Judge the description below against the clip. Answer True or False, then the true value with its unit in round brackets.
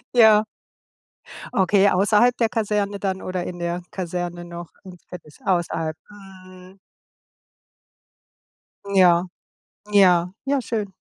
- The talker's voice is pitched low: False (185 Hz)